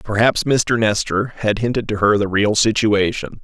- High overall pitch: No, low, 105 Hz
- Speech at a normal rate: Yes, average, 175 wpm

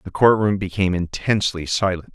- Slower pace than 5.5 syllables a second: No, 5.9 syllables/s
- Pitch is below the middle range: Yes, very low, 95 Hz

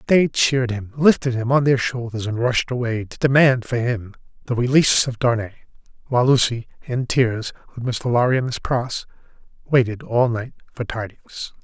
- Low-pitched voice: Yes, low, 120 Hz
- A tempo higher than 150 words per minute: Yes, average, 175 wpm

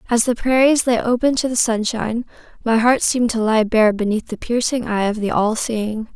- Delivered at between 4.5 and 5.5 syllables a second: Yes, 5.3 syllables/s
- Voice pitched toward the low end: No, high, 230 Hz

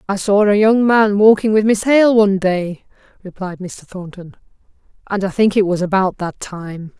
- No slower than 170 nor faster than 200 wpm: Yes, average, 190 wpm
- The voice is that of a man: No, female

